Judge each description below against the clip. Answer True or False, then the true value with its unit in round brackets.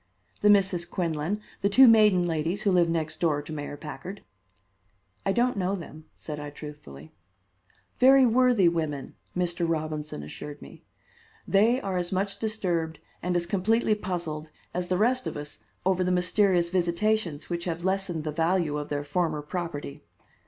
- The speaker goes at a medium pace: True (160 wpm)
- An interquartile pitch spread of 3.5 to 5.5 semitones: True (4.2 semitones)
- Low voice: False (175 Hz)